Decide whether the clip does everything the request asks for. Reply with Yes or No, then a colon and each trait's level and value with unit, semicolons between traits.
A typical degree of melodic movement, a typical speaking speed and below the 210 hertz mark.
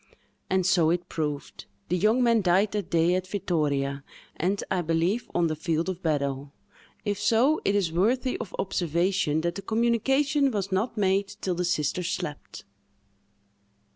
Yes: average, 4.1 semitones; average, 160 wpm; medium, 185 Hz